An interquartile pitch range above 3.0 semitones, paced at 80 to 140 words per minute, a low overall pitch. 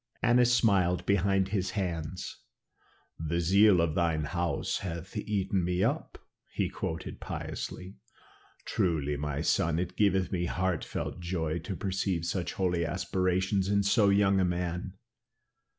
No: narrow, 2.5 semitones; slow, 135 wpm; very low, 90 Hz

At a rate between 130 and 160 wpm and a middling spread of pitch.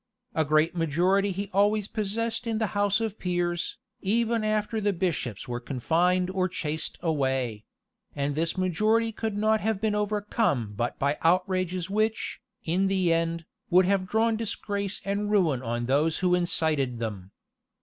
Yes: average, 155 wpm; average, 4.7 semitones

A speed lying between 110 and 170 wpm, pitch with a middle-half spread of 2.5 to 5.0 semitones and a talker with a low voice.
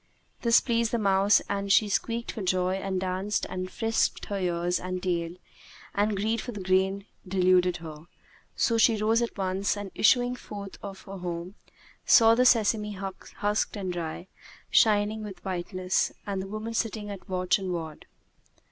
No: average, 165 wpm; average, 2.8 semitones; high, 195 Hz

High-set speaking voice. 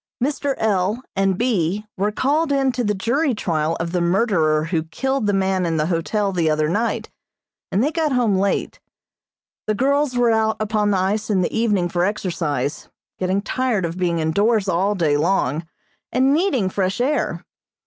Yes: high, 200 Hz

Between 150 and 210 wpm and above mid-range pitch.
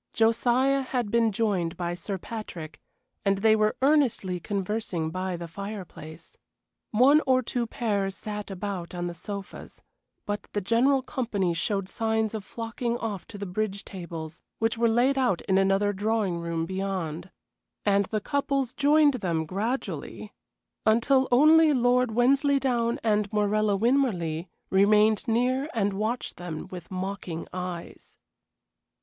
No: average, 140 wpm; high, 210 Hz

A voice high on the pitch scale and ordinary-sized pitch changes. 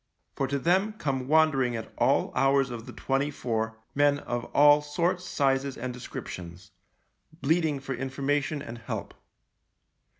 No: low, 135 Hz; average, 3.0 semitones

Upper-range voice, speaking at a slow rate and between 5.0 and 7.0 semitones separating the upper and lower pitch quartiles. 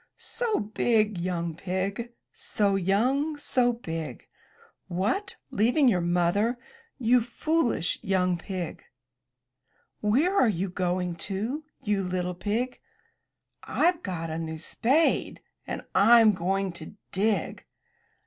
Yes: high, 200 Hz; slow, 115 wpm; average, 5.3 semitones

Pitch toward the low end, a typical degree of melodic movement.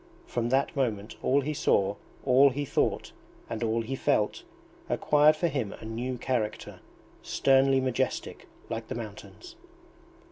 Yes: low, 130 Hz; average, 3.4 semitones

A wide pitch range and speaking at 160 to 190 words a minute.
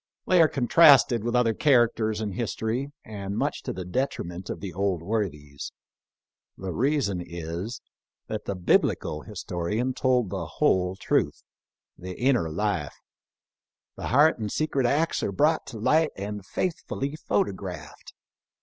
No: wide, 6.0 semitones; average, 140 wpm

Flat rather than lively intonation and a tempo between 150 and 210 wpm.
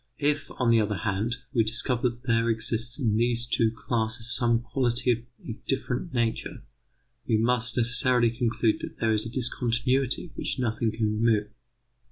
Yes: narrow, 1.7 semitones; average, 165 wpm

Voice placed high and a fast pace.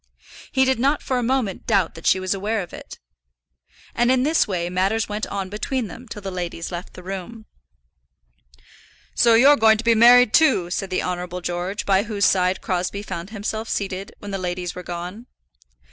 No: high, 200 Hz; average, 190 wpm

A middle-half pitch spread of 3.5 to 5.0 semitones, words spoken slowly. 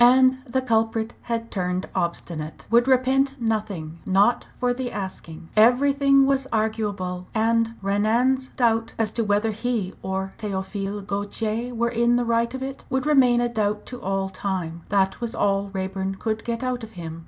No: average, 3.9 semitones; average, 165 wpm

